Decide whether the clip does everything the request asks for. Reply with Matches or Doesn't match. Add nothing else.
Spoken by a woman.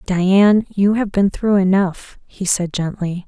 Matches